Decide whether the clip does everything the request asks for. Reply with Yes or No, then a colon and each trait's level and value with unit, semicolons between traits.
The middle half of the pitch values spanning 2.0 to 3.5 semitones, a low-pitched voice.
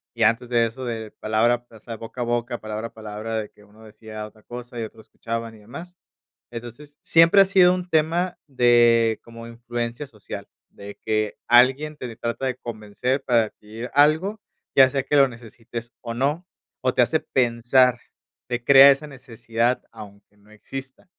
Yes: average, 3.1 semitones; low, 120 Hz